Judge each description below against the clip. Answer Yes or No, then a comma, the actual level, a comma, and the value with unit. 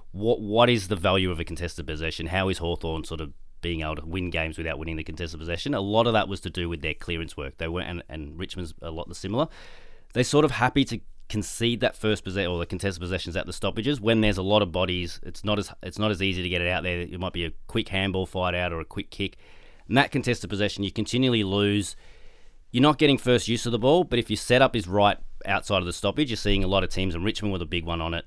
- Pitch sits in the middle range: No, very low, 95 Hz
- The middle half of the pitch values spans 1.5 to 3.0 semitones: No, average, 4.0 semitones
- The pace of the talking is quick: Yes, fast, 275 wpm